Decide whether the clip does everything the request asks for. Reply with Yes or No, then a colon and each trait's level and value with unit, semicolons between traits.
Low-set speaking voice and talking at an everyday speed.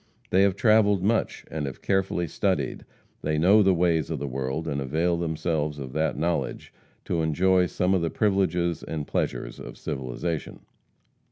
Yes: very low, 85 Hz; average, 165 wpm